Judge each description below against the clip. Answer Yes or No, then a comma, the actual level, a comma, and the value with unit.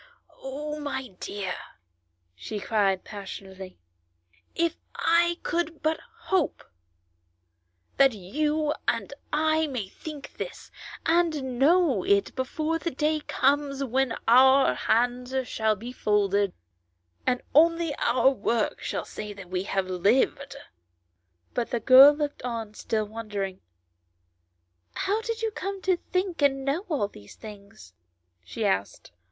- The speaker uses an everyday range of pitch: No, wide, 7.3 semitones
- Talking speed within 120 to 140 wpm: Yes, slow, 135 wpm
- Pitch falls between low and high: No, very high, 255 Hz